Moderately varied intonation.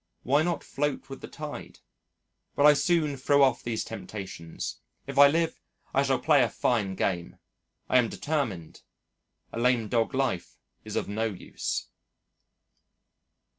Yes: average, 4.3 semitones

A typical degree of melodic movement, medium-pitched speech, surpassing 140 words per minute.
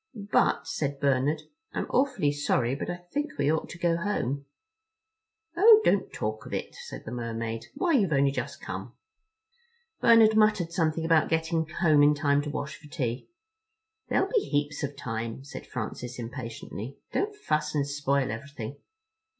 Yes: average, 4.2 semitones; medium, 145 Hz; average, 160 wpm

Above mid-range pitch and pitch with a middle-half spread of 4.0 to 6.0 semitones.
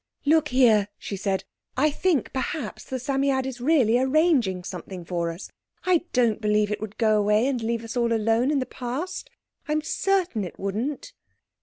Yes: high, 245 Hz; average, 5.0 semitones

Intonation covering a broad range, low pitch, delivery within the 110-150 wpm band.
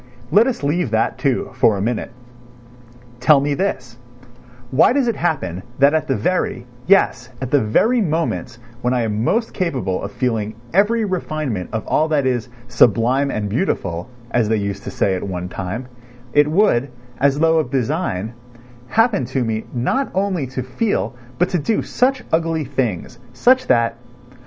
No: wide, 6.8 semitones; low, 130 Hz; average, 170 wpm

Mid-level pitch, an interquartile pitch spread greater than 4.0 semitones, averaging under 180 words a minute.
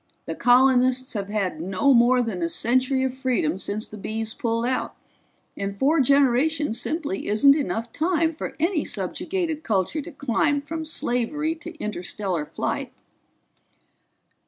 No: very high, 255 Hz; wide, 5.6 semitones; average, 140 wpm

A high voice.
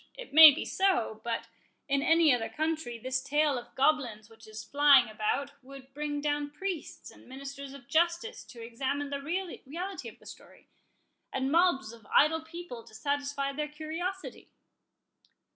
Yes: very high, 280 Hz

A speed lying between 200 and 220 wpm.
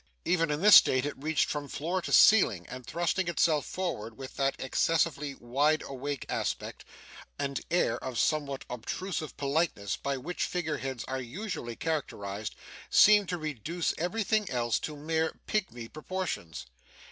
No: average, 145 wpm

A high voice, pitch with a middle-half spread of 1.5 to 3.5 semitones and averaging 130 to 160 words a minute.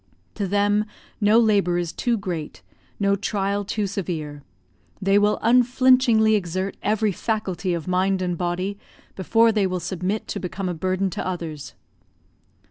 Yes: high, 195 Hz; average, 2.7 semitones; average, 145 wpm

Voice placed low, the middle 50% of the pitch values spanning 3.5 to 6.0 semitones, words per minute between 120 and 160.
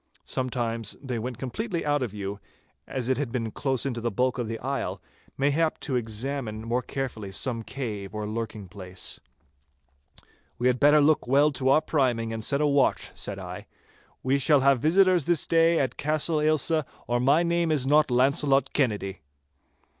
No: low, 130 Hz; average, 4.3 semitones; average, 175 wpm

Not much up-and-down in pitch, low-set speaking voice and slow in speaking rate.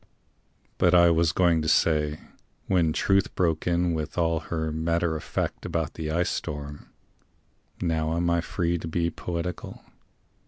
No: narrow, 1.5 semitones; very low, 85 Hz; average, 155 wpm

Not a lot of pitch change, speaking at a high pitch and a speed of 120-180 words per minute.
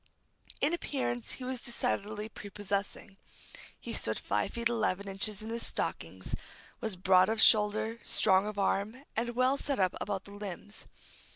No: average, 3.0 semitones; high, 210 Hz; average, 155 wpm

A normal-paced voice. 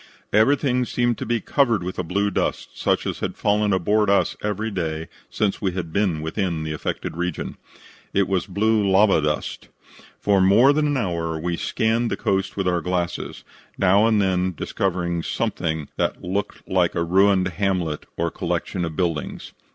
Yes: average, 175 wpm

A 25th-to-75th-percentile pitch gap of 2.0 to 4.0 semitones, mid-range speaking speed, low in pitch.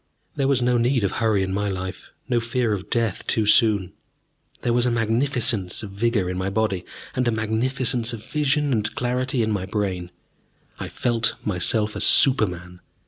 Yes: average, 3.7 semitones; average, 185 wpm; low, 110 Hz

